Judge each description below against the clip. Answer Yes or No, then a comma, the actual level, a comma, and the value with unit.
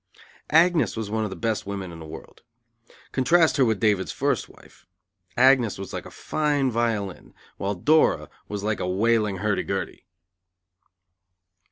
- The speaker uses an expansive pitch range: No, average, 5.0 semitones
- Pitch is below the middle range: Yes, low, 110 Hz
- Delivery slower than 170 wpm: Yes, average, 155 wpm